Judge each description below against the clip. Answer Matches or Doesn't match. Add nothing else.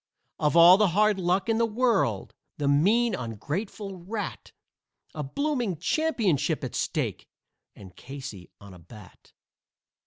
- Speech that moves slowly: Matches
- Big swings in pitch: Matches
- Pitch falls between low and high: Matches